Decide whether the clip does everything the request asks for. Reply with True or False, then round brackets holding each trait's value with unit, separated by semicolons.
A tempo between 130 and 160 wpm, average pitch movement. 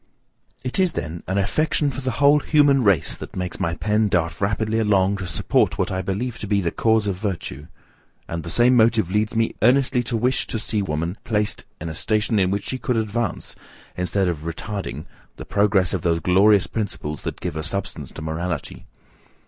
False (195 wpm; 4.3 semitones)